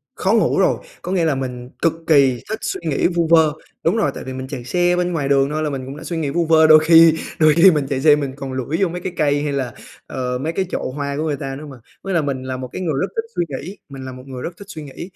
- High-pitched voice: No, medium, 150 Hz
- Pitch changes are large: No, average, 3.7 semitones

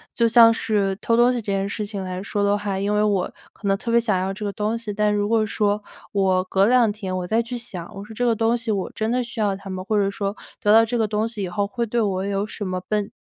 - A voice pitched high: Yes, high, 210 Hz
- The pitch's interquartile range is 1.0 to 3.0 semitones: Yes, narrow, 2.5 semitones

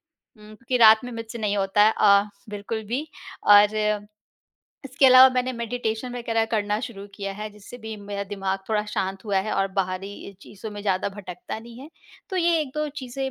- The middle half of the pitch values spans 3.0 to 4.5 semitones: Yes, average, 3.3 semitones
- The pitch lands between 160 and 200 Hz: No, high, 215 Hz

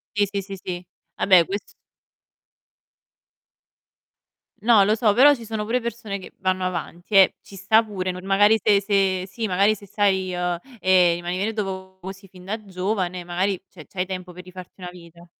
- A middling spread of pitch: No, narrow, 2.2 semitones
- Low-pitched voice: No, high, 190 Hz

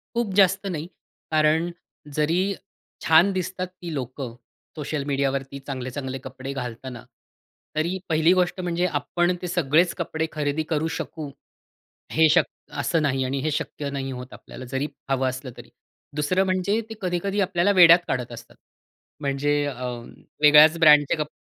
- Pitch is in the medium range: Yes, medium, 155 Hz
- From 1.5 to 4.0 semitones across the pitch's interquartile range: No, average, 4.4 semitones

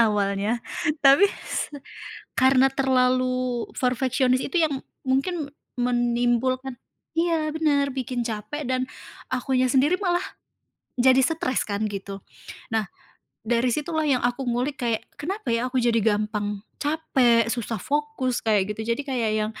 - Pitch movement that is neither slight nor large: Yes, average, 3.1 semitones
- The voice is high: Yes, very high, 255 Hz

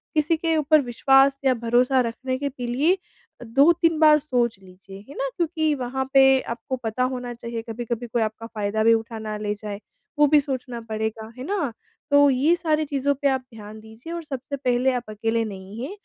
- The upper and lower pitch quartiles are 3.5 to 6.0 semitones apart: Yes, average, 4.1 semitones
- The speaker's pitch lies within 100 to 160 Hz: No, very high, 250 Hz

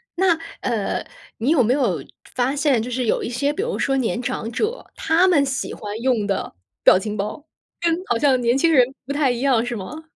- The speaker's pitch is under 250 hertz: No, very high, 255 Hz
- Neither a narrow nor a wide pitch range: Yes, average, 4.2 semitones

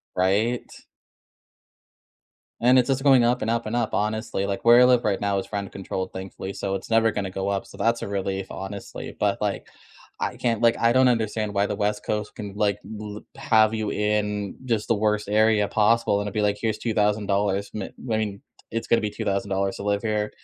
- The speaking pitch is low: Yes, low, 105 Hz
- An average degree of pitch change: No, narrow, 2.1 semitones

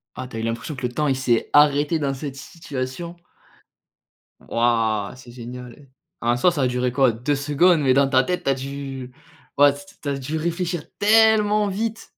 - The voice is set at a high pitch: No, medium, 140 Hz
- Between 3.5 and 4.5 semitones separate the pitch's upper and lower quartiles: Yes, average, 4.1 semitones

